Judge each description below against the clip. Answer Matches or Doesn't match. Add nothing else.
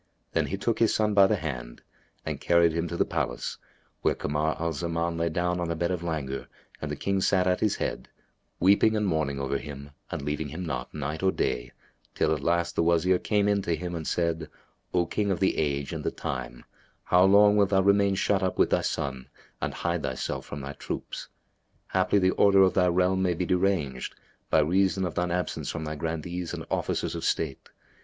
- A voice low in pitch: Matches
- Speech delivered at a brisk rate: Matches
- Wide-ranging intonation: Doesn't match